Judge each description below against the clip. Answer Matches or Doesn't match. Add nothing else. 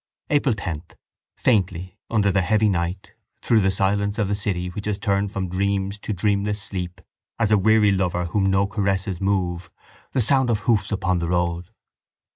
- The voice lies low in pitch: Matches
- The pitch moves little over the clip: Matches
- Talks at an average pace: Matches